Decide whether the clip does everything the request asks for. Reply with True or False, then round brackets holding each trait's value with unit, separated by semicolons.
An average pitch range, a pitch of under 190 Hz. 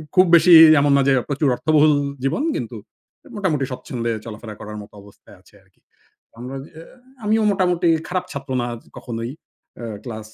False (6.5 semitones; 140 Hz)